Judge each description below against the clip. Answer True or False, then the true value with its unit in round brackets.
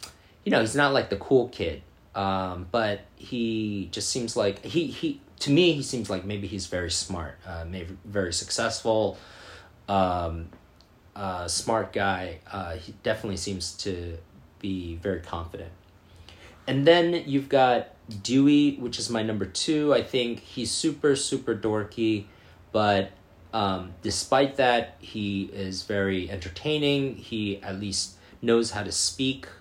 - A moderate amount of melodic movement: True (4.0 semitones)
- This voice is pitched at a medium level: False (100 Hz)